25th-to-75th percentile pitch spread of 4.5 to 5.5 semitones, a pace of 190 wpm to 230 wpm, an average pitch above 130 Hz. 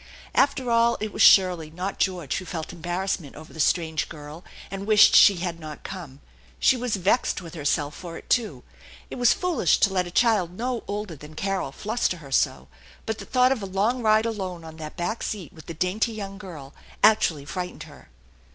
Yes: average, 5.0 semitones; fast, 205 wpm; medium, 185 Hz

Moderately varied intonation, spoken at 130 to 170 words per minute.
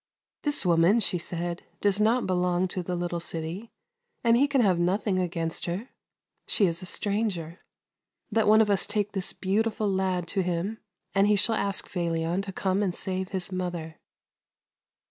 No: average, 3.0 semitones; average, 180 wpm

